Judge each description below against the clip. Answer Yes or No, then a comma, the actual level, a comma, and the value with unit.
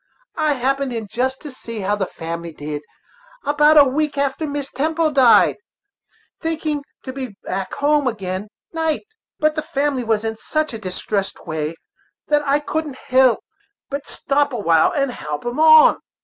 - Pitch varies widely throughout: Yes, wide, 5.7 semitones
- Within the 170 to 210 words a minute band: No, average, 160 wpm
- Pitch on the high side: Yes, very high, 270 Hz